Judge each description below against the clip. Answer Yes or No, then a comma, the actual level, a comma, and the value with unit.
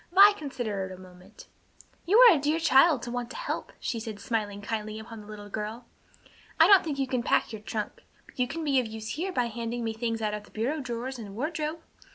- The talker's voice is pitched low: No, high, 235 Hz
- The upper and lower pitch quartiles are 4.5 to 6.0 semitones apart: Yes, wide, 5.5 semitones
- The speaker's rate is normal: No, fast, 230 wpm